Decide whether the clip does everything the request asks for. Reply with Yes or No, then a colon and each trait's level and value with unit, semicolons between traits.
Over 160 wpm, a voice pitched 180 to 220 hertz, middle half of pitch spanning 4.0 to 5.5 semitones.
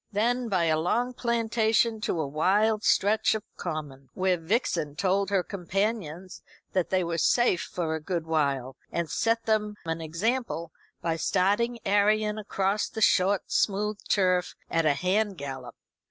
No: average, 155 wpm; high, 190 Hz; average, 4.6 semitones